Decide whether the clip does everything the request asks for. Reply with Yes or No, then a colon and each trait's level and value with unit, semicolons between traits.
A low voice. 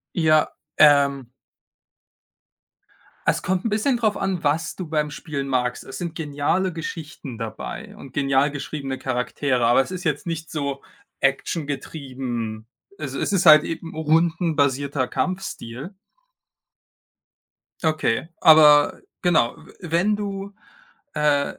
No: medium, 150 Hz